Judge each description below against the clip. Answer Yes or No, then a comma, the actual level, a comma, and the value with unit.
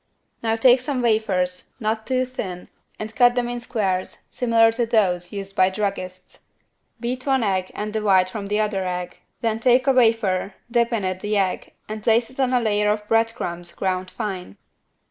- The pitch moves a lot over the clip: No, average, 3.9 semitones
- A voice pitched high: Yes, high, 215 Hz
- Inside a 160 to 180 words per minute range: No, average, 190 wpm